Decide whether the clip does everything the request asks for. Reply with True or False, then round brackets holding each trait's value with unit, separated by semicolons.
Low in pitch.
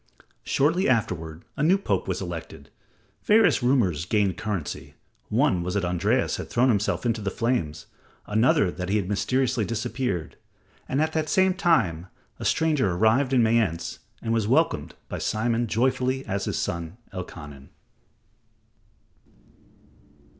True (110 Hz)